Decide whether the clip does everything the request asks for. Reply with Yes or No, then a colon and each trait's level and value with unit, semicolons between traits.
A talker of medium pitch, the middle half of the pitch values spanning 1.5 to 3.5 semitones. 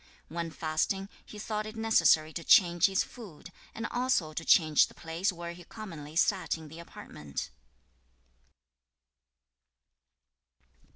No: medium, 170 Hz; average, 4.6 semitones